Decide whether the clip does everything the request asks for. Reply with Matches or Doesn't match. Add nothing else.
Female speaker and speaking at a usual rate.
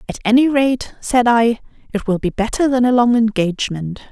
Matches